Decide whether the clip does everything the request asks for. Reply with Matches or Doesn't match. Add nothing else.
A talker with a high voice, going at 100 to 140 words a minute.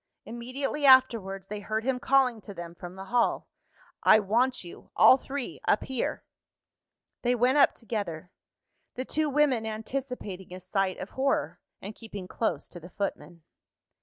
Doesn't match